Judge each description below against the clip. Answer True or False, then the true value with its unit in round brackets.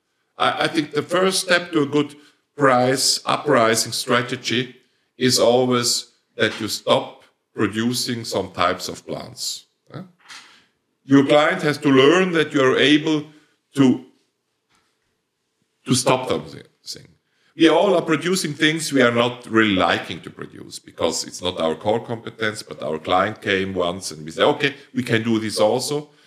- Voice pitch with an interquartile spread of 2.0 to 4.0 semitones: False (4.5 semitones)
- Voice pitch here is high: False (130 Hz)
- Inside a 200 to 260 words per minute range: False (150 wpm)